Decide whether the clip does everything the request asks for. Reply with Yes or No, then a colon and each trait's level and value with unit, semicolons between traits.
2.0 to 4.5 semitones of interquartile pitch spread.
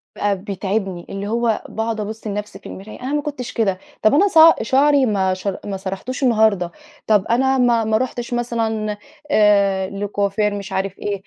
Yes: average, 3.1 semitones